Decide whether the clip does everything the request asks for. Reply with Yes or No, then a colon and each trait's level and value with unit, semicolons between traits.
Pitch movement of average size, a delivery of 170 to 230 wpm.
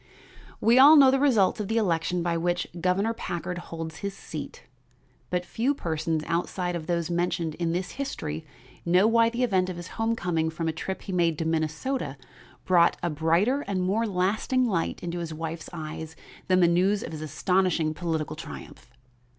Yes: average, 3.7 semitones; average, 180 wpm